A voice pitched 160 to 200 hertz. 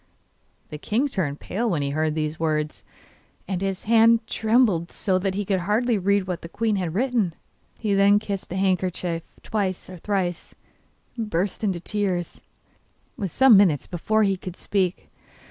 Yes: high, 190 Hz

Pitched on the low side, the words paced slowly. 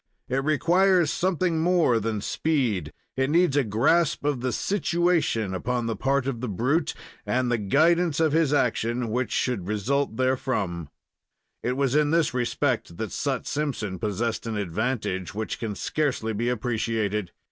No: low, 125 Hz; average, 155 wpm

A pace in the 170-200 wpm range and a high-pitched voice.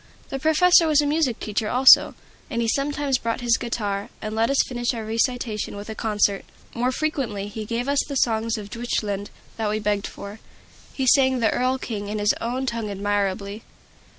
Yes: average, 190 wpm; high, 230 Hz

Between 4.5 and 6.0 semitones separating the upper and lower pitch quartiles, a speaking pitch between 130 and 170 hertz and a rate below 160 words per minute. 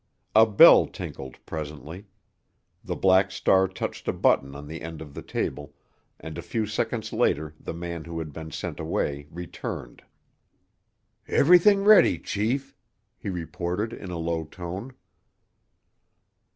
No: average, 5.0 semitones; very low, 85 Hz; average, 140 wpm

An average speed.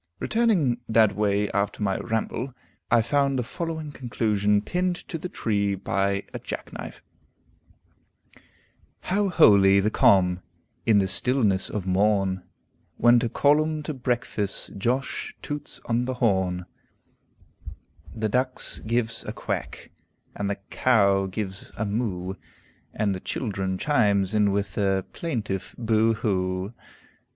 No: slow, 130 wpm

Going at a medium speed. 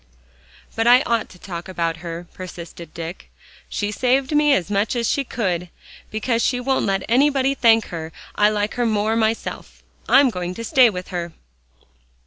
Yes: average, 170 wpm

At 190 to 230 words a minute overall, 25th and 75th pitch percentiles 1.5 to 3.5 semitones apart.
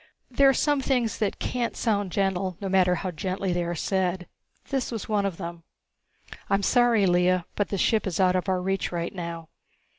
Yes: average, 200 wpm; average, 2.9 semitones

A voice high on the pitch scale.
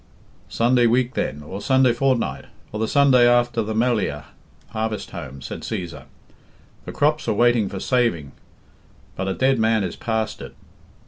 No: low, 115 Hz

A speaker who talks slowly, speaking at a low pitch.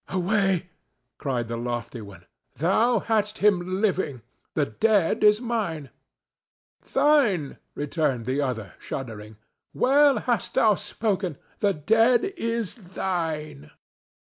No: slow, 110 wpm; medium, 180 Hz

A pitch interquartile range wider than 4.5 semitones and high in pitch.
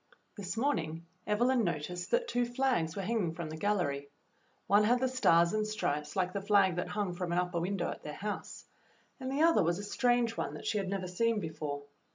Yes: average, 5.2 semitones; high, 195 Hz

